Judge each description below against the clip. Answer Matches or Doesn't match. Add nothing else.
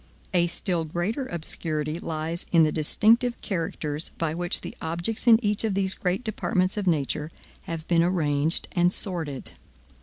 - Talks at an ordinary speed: Matches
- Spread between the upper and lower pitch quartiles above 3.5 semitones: Doesn't match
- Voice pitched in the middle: Matches